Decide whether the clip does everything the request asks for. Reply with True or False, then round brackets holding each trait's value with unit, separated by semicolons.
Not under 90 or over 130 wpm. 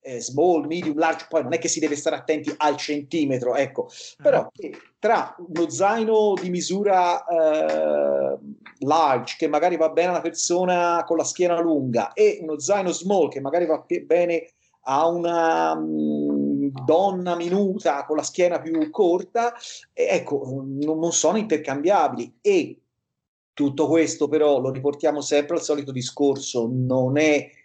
False (145 wpm)